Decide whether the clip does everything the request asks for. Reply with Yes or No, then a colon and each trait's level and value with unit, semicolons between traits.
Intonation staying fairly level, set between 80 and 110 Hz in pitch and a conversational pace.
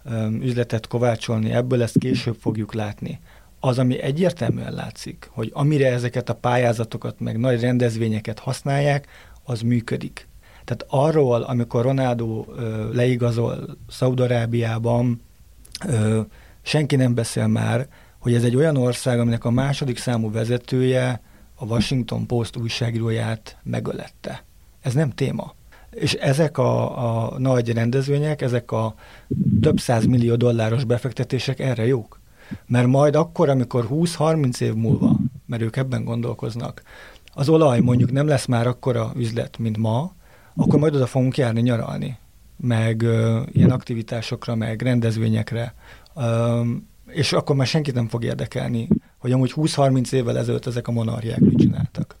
No: narrow, 2.3 semitones; low, 120 Hz; average, 135 wpm